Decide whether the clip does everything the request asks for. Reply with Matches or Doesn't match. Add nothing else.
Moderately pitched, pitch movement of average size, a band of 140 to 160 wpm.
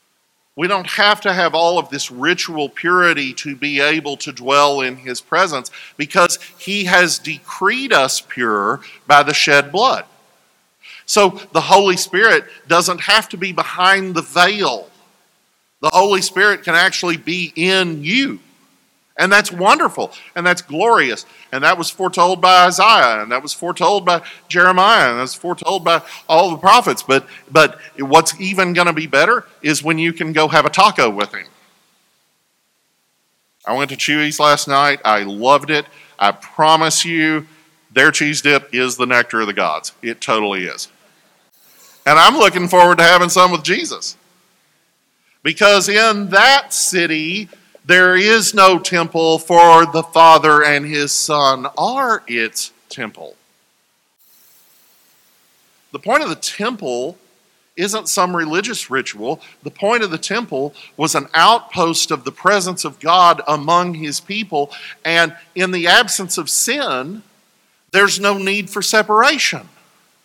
Matches